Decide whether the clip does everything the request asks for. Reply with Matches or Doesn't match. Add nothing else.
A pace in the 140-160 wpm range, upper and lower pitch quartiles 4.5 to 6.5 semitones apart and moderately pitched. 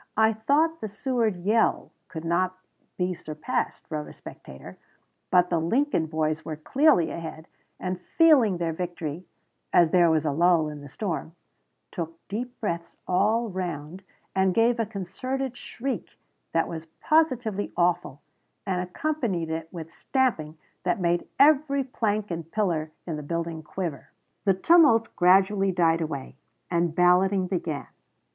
Matches